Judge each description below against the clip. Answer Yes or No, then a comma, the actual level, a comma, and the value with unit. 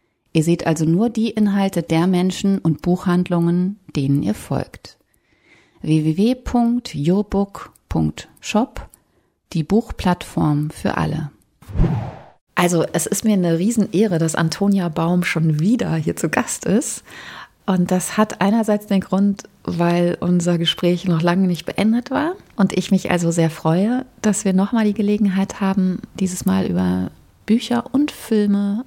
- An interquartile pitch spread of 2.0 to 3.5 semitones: No, average, 3.9 semitones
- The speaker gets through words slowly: No, average, 135 wpm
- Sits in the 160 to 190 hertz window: Yes, medium, 185 Hz